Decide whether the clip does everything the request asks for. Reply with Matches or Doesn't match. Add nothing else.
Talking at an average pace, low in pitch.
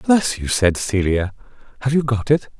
Matches